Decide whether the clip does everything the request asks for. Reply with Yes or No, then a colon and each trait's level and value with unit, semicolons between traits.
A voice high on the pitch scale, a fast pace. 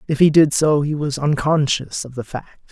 No: medium, 145 Hz; fast, 220 wpm